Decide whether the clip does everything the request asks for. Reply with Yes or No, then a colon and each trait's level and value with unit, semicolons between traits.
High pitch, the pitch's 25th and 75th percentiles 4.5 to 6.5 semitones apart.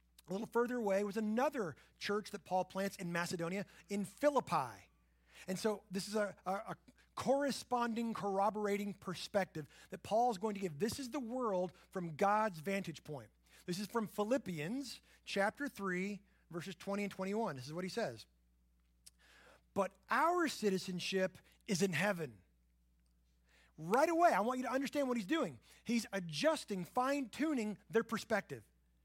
Yes: high, 200 Hz; average, 4.9 semitones